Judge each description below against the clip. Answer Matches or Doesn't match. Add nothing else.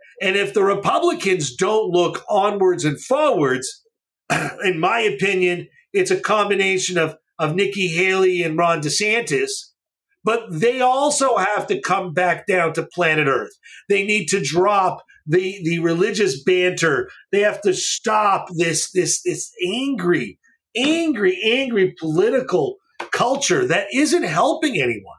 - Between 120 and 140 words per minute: Matches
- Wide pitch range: Matches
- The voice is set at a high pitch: Matches